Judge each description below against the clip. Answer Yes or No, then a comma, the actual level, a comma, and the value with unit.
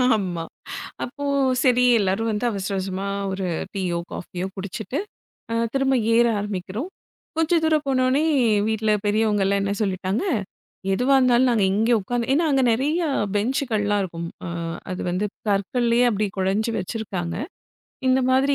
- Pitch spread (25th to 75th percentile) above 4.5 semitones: Yes, average, 4.9 semitones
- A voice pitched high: Yes, high, 215 Hz